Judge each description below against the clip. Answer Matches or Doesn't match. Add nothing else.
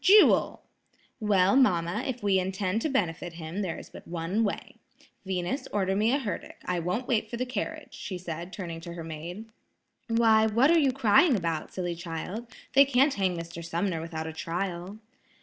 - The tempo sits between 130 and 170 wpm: Doesn't match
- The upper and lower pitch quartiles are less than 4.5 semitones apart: Doesn't match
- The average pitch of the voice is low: Doesn't match